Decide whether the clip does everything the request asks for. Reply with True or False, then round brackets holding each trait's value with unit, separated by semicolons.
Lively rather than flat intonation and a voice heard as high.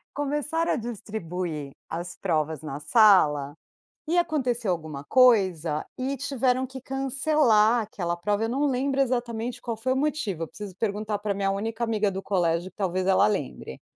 True (6.5 semitones; 215 Hz)